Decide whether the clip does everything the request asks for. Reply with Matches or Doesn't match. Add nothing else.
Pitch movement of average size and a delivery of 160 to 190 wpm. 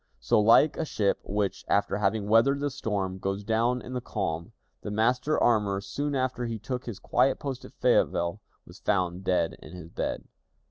Matches